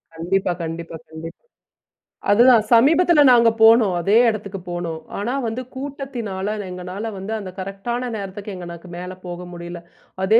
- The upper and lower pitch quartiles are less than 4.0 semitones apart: No, average, 4.6 semitones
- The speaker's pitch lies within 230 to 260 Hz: No, high, 195 Hz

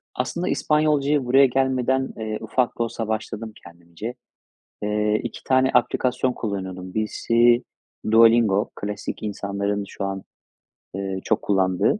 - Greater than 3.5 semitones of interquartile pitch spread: Yes, average, 4.1 semitones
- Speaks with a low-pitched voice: Yes, low, 110 Hz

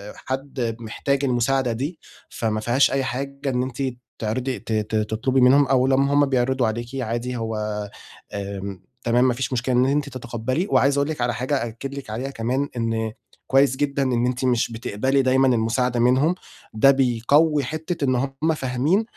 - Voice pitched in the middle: No, low, 130 Hz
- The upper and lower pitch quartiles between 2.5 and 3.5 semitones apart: Yes, average, 2.8 semitones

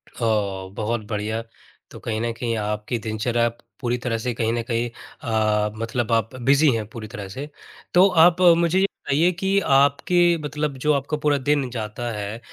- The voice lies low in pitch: Yes, low, 120 Hz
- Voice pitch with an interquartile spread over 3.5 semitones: Yes, average, 5.1 semitones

